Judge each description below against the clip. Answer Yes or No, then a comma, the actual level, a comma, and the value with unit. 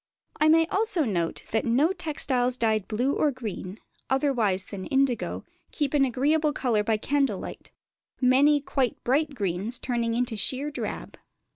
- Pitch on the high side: Yes, very high, 255 Hz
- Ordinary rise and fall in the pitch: Yes, average, 4.6 semitones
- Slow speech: No, average, 155 wpm